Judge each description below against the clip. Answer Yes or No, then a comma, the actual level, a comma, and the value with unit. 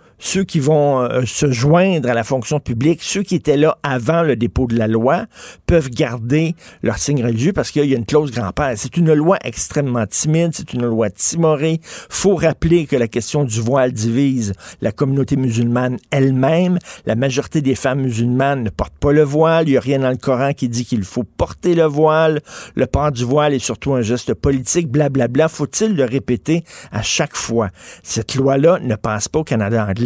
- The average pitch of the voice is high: No, low, 135 Hz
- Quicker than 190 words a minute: Yes, average, 205 wpm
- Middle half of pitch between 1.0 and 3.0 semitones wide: No, average, 4.4 semitones